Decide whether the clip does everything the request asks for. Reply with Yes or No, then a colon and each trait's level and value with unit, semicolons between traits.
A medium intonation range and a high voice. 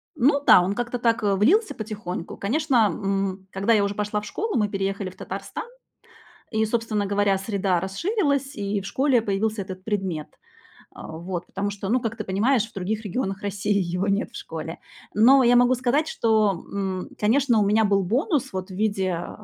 Yes: average, 3.4 semitones; high, 205 Hz